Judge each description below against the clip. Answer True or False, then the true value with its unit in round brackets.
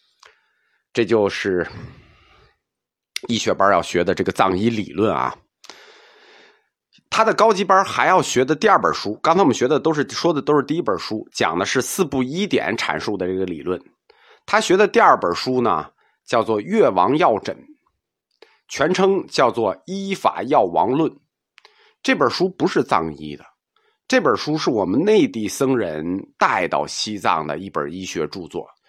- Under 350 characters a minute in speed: True (230 characters per minute)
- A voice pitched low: False (190 Hz)